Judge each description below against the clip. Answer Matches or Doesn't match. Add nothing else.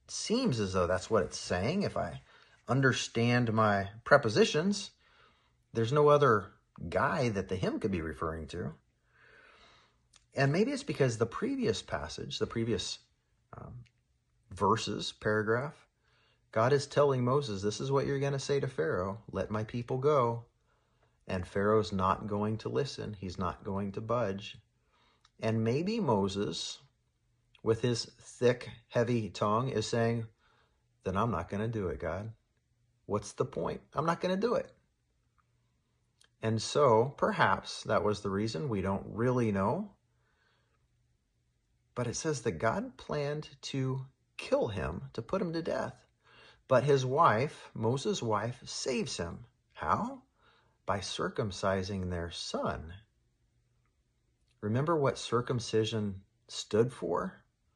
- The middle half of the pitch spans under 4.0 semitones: Matches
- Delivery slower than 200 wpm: Matches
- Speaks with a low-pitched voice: Matches